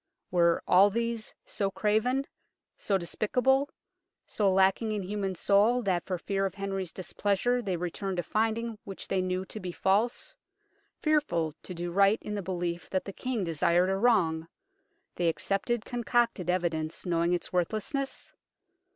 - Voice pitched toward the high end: Yes, high, 195 Hz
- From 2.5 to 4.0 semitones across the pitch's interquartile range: Yes, average, 3.6 semitones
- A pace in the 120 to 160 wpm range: Yes, average, 150 wpm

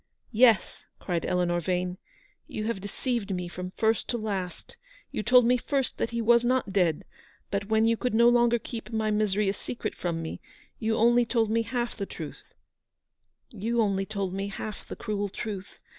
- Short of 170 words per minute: No, average, 195 wpm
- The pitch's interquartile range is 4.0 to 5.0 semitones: No, average, 3.3 semitones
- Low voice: No, high, 215 Hz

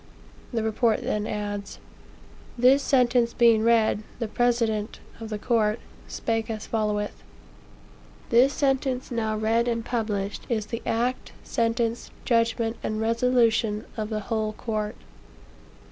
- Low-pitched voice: No, high, 225 Hz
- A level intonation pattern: Yes, narrow, 1.7 semitones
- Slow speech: Yes, slow, 125 wpm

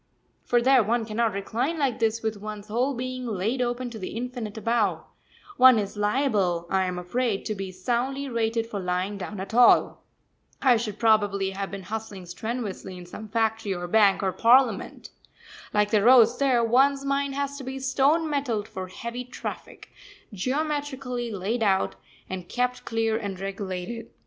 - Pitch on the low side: No, high, 225 Hz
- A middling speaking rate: Yes, average, 170 wpm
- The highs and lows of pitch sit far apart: No, average, 4.0 semitones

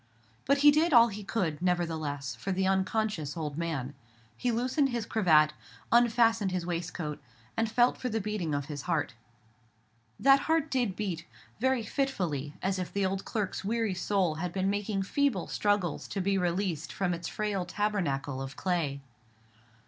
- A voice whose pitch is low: No, high, 190 Hz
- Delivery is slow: No, average, 165 wpm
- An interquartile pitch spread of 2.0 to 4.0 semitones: No, average, 5.1 semitones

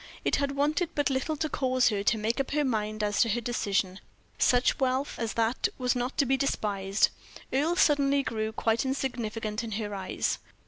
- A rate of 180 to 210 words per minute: Yes, average, 190 wpm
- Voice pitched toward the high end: Yes, high, 245 Hz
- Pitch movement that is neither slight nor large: Yes, average, 4.3 semitones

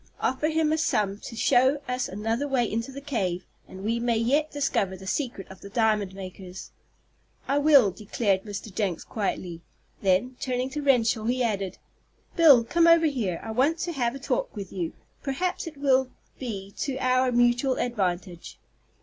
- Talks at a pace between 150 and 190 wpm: Yes, average, 175 wpm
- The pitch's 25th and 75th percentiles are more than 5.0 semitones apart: Yes, wide, 5.4 semitones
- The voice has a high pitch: Yes, high, 240 Hz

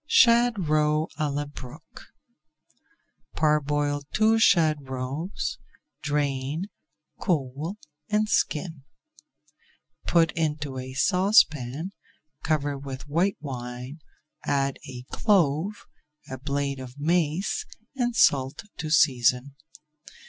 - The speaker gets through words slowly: Yes, slow, 95 wpm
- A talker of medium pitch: Yes, medium, 150 Hz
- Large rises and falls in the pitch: No, average, 3.8 semitones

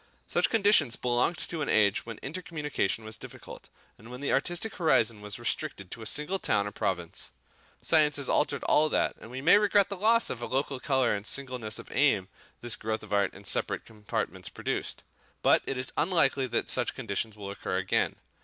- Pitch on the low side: Yes, low, 130 Hz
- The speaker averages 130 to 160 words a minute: No, average, 190 wpm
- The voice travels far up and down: Yes, wide, 6.2 semitones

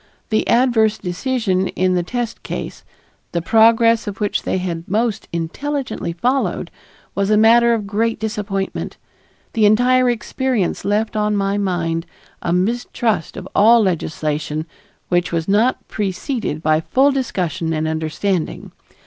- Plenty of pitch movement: No, average, 4.7 semitones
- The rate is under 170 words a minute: Yes, slow, 135 wpm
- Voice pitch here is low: No, high, 205 Hz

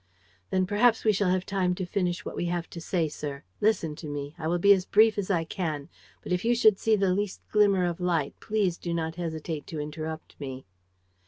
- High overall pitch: No, medium, 180 Hz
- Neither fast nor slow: No, fast, 225 wpm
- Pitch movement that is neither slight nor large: Yes, average, 3.8 semitones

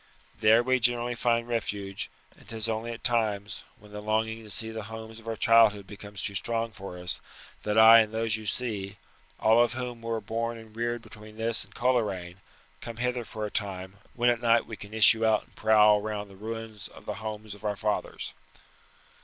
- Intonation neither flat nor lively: No, narrow, 1.7 semitones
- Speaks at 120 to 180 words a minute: No, fast, 205 wpm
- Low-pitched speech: Yes, low, 110 Hz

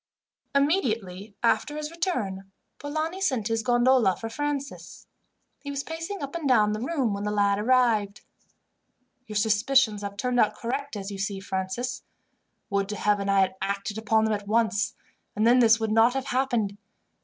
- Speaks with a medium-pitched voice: No, high, 225 Hz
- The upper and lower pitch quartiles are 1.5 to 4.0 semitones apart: No, average, 4.7 semitones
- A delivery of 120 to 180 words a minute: Yes, average, 170 wpm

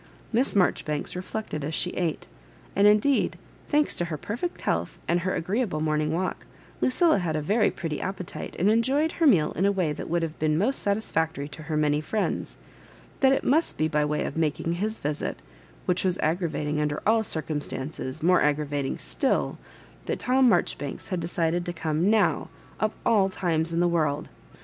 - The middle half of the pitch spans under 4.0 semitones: No, average, 5.3 semitones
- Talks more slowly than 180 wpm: No, average, 185 wpm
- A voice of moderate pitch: Yes, medium, 175 Hz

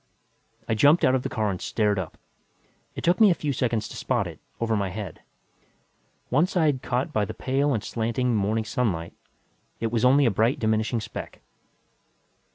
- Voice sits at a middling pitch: No, low, 115 Hz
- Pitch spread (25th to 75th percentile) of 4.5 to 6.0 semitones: No, average, 3.5 semitones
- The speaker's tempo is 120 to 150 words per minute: No, average, 180 wpm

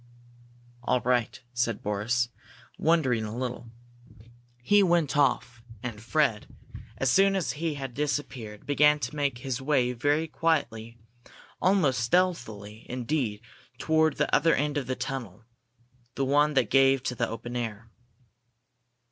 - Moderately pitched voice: No, low, 130 Hz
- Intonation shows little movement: No, average, 4.0 semitones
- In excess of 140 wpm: No, slow, 135 wpm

